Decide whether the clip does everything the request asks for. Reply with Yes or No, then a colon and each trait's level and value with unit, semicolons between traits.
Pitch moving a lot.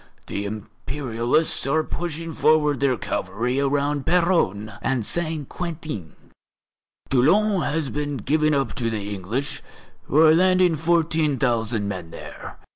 Yes: wide, 5.7 semitones